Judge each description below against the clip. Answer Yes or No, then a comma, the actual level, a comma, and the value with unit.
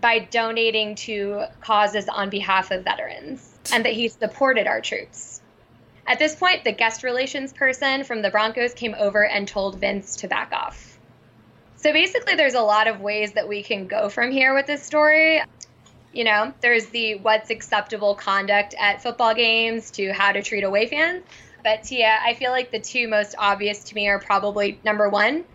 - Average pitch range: Yes, average, 3.1 semitones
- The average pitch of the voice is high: Yes, high, 220 Hz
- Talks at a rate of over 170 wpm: Yes, average, 185 wpm